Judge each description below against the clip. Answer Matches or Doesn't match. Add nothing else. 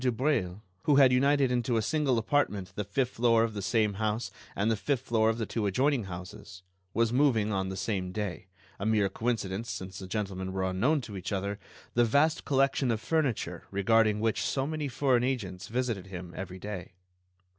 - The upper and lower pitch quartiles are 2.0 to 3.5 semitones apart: Doesn't match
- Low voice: Matches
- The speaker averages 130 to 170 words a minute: Doesn't match